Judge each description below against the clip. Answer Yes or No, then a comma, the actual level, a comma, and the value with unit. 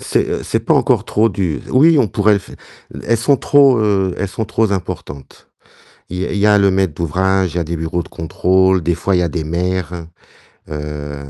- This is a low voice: Yes, very low, 95 Hz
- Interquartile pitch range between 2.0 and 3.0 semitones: No, average, 3.7 semitones